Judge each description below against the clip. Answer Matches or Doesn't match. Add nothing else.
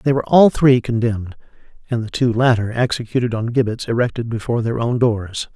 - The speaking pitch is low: Matches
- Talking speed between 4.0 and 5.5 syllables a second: Doesn't match